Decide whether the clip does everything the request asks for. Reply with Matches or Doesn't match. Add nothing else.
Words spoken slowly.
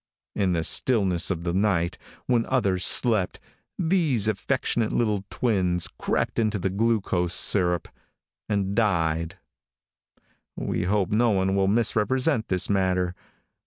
Matches